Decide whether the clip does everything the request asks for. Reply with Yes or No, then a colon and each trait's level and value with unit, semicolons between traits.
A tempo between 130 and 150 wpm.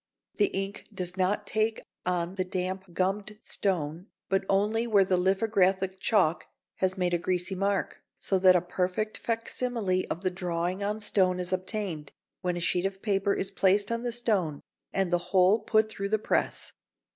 No: average, 175 wpm